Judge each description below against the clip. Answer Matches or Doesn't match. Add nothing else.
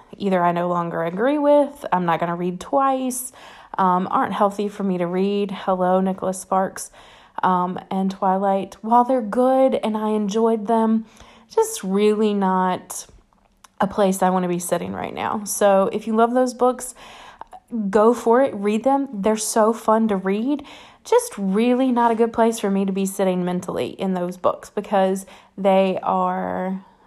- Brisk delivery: Doesn't match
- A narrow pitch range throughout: Doesn't match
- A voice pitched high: Matches